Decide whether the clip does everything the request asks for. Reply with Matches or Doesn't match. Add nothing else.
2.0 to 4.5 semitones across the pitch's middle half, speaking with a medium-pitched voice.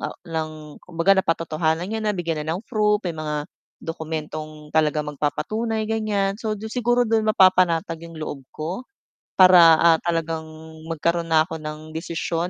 Matches